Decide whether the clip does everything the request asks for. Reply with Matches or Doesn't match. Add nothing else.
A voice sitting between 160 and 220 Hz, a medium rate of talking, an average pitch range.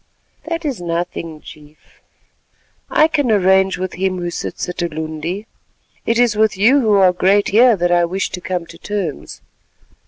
Matches